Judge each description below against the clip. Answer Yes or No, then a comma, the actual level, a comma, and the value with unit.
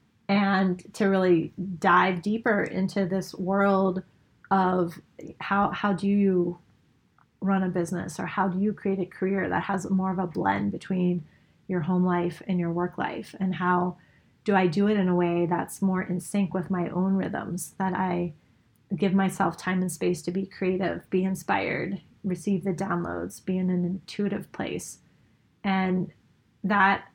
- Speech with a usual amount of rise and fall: No, narrow, 1.6 semitones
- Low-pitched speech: No, medium, 185 Hz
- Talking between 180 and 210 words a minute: No, average, 170 wpm